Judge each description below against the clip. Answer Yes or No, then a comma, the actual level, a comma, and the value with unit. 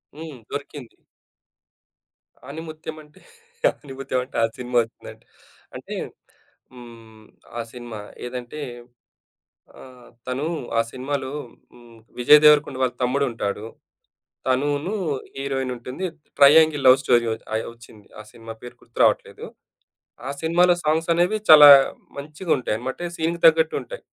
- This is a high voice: No, low, 135 Hz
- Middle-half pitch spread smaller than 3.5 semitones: No, average, 4.1 semitones